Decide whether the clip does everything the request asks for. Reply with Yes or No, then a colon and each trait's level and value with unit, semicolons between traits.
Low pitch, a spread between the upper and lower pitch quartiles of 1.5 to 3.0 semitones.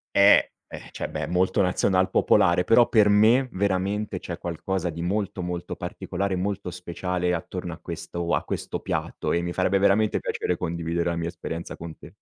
Yes: very low, 90 Hz; narrow, 2.5 semitones